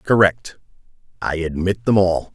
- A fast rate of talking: No, slow, 130 wpm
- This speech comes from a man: Yes, male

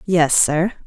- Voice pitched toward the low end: No, medium, 170 Hz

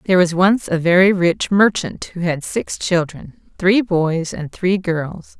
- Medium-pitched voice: Yes, medium, 180 Hz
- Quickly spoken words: No, average, 180 wpm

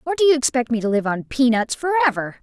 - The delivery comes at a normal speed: No, fast, 250 wpm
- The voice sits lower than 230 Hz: No, very high, 260 Hz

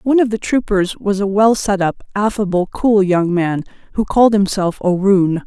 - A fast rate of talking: No, average, 185 wpm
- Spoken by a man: No, female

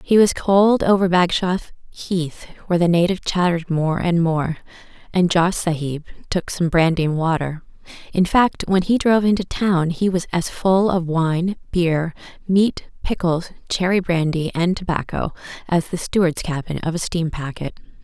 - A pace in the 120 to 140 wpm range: No, average, 165 wpm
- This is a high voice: No, medium, 175 Hz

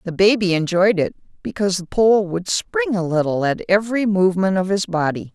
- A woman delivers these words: Yes, female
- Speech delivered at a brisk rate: No, average, 190 wpm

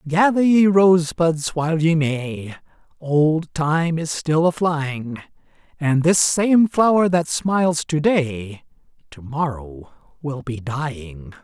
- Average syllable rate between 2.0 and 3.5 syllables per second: Yes, 3.3 syllables/s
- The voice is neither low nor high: Yes, medium, 155 Hz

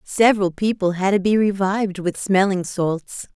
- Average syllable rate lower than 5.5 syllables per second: Yes, 4.7 syllables/s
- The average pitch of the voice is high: Yes, high, 195 Hz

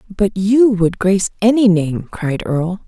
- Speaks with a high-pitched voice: Yes, high, 195 Hz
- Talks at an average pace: Yes, average, 165 wpm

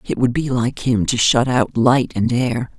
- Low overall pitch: Yes, low, 120 Hz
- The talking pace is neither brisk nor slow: No, fast, 235 wpm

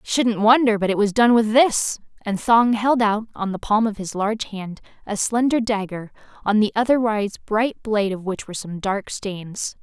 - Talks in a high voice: Yes, high, 215 Hz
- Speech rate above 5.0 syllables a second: No, 4.8 syllables/s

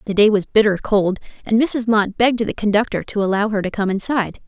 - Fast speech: Yes, fast, 230 wpm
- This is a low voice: No, high, 210 Hz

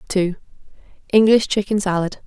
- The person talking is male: No, female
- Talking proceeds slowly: Yes, slow, 80 wpm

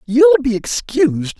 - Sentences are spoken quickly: No, slow, 130 wpm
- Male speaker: Yes, male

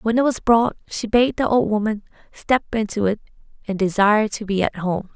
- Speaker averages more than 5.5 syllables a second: No, 5.2 syllables/s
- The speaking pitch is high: Yes, high, 215 Hz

